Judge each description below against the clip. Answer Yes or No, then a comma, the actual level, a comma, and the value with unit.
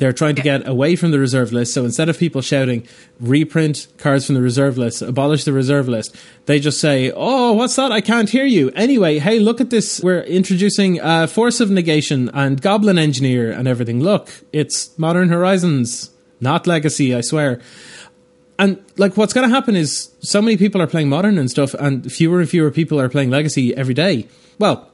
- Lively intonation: Yes, wide, 6.0 semitones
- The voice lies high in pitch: No, medium, 150 Hz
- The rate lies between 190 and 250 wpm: Yes, average, 200 wpm